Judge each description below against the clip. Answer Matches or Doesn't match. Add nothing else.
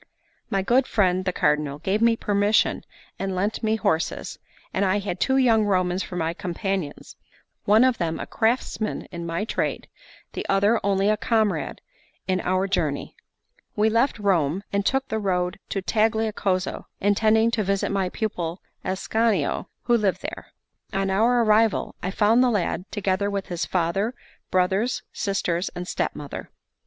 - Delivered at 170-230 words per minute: Doesn't match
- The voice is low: Doesn't match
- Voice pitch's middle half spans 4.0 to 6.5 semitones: Doesn't match